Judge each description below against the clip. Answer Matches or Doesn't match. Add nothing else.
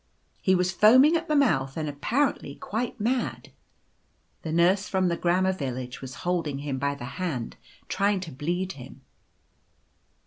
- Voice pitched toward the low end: Doesn't match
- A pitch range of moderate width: Doesn't match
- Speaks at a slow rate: Doesn't match